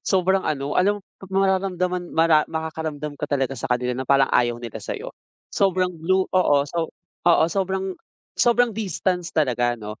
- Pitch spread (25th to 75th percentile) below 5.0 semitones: No, wide, 5.5 semitones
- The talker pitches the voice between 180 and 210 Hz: No, medium, 165 Hz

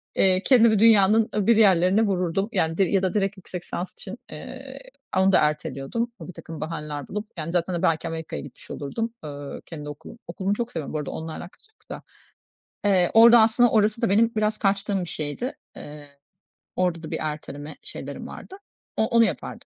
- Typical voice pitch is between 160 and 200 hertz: Yes, high, 190 Hz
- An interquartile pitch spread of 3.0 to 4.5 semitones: No, average, 5.2 semitones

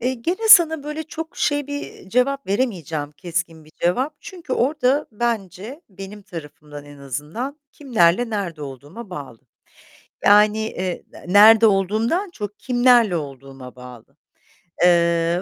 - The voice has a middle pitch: No, high, 205 Hz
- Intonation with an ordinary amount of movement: No, wide, 7.5 semitones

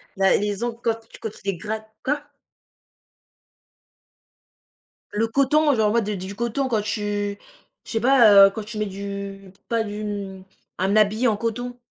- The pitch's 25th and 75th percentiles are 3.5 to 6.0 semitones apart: No, narrow, 2.6 semitones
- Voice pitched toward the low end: No, high, 215 Hz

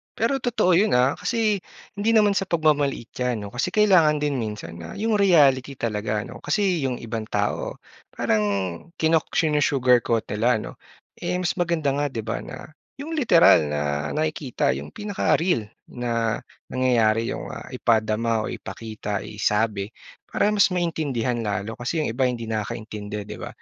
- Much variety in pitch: Yes, wide, 7.5 semitones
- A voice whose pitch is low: Yes, low, 125 Hz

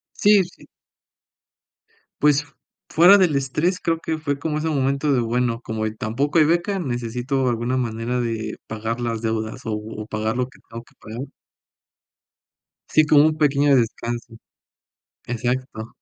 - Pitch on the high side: No, low, 125 Hz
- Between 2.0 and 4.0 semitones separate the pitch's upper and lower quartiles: No, average, 4.5 semitones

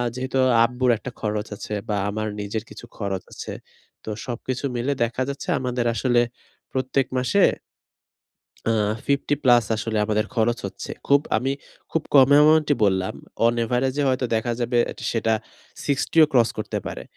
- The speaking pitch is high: No, low, 120 Hz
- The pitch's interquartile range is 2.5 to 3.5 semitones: Yes, average, 3.1 semitones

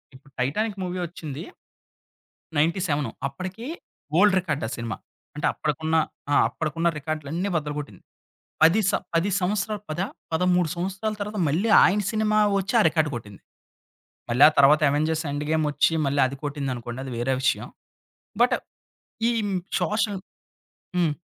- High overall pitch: No, medium, 160 Hz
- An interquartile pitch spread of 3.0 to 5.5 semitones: Yes, average, 5.2 semitones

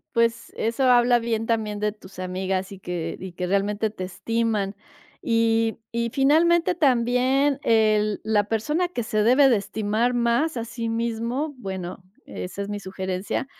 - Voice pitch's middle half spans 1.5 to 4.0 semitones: Yes, average, 3.1 semitones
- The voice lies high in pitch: Yes, high, 225 Hz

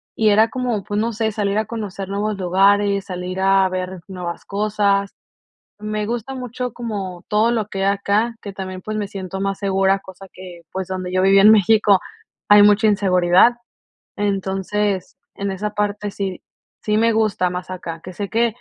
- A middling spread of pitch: No, narrow, 2.0 semitones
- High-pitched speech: Yes, high, 200 Hz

